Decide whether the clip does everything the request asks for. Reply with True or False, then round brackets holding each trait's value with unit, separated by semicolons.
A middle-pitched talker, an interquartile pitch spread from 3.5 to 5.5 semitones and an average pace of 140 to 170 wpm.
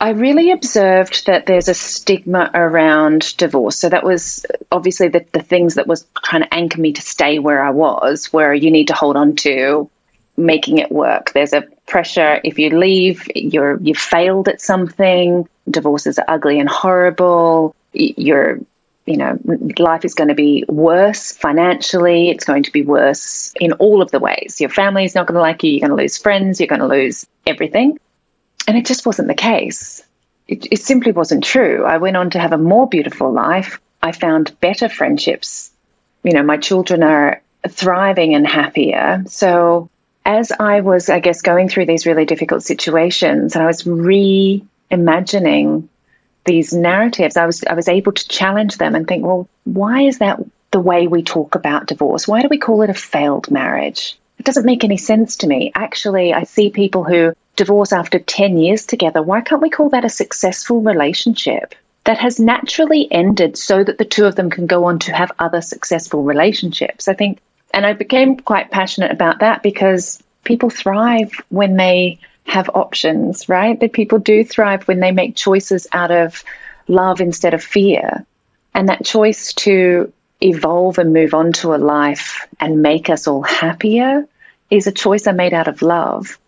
False (180 Hz; 3.9 semitones; 185 wpm)